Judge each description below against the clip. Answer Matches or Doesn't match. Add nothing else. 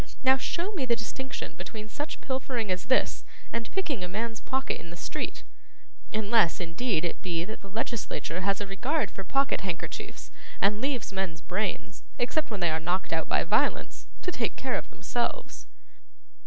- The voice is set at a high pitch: Matches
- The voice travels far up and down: Matches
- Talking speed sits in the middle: Matches